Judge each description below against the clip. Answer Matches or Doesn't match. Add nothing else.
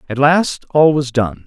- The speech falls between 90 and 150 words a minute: Doesn't match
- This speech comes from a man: Matches